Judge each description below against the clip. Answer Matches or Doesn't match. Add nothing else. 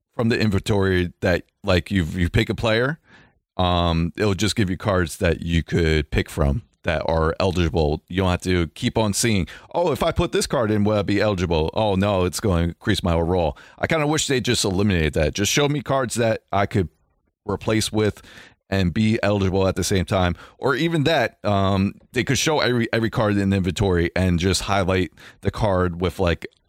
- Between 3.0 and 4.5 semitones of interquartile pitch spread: Matches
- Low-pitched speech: Matches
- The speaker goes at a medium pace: Doesn't match